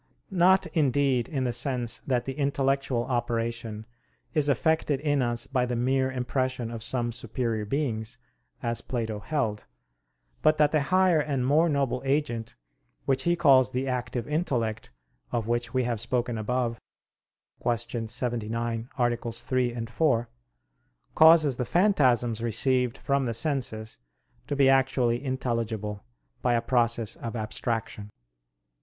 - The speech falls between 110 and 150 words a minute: Yes, slow, 135 wpm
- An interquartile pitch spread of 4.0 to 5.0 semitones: No, average, 2.8 semitones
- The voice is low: Yes, low, 125 Hz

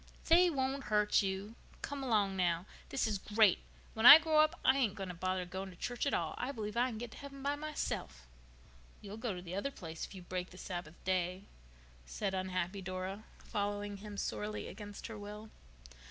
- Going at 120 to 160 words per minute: No, average, 200 wpm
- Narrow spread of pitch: No, average, 4.6 semitones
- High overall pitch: Yes, high, 205 Hz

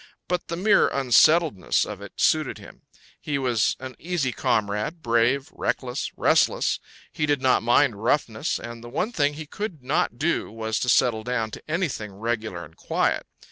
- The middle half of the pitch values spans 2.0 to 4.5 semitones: No, average, 5.1 semitones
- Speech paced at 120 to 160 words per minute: No, average, 170 wpm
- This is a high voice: No, low, 125 Hz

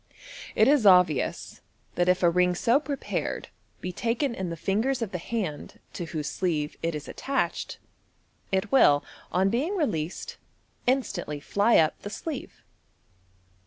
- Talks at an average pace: Yes, average, 145 wpm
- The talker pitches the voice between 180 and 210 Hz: Yes, high, 190 Hz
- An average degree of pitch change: No, wide, 6.1 semitones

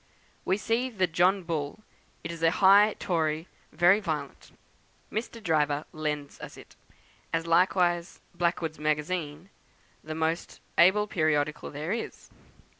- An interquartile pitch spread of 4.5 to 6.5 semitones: No, average, 3.4 semitones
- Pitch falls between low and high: Yes, medium, 170 Hz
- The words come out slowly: Yes, slow, 125 wpm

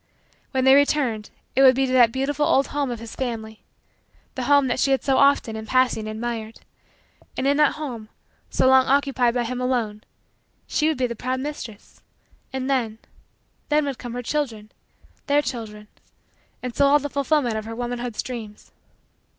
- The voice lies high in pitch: Yes, very high, 255 Hz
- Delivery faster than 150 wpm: Yes, average, 180 wpm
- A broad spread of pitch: No, average, 3.3 semitones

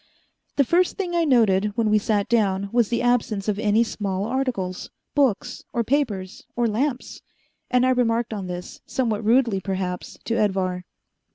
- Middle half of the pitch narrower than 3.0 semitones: No, average, 3.9 semitones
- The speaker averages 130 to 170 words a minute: Yes, average, 165 wpm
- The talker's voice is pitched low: No, high, 220 Hz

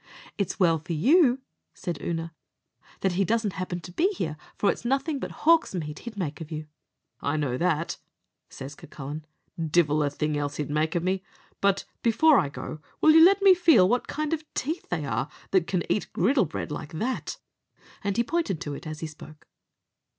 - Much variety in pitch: Yes, wide, 7.9 semitones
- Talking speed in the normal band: Yes, average, 195 wpm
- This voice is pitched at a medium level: Yes, medium, 175 Hz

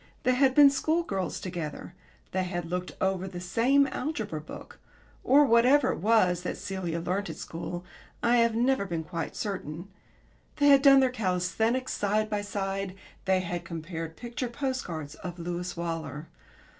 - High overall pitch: Yes, high, 195 Hz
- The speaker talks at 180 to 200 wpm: No, average, 160 wpm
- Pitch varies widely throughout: Yes, wide, 5.9 semitones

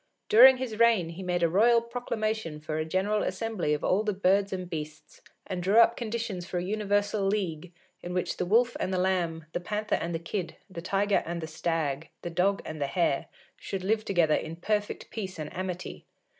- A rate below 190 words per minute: No, fast, 205 wpm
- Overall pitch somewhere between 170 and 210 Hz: Yes, medium, 185 Hz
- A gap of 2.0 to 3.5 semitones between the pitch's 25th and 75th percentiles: No, average, 4.1 semitones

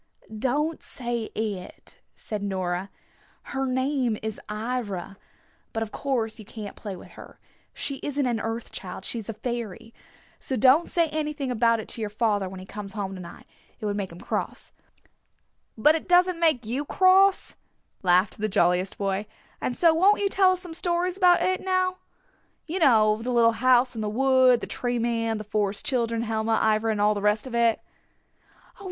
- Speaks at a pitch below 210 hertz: No, high, 230 Hz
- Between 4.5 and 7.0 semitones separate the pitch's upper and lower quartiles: Yes, average, 4.9 semitones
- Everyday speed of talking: Yes, average, 185 wpm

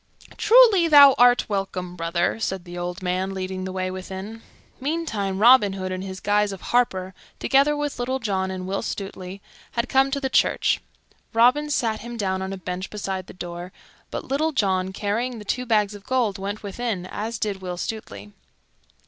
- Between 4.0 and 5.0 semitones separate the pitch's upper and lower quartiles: Yes, average, 4.5 semitones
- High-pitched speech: Yes, high, 200 Hz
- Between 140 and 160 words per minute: No, average, 180 wpm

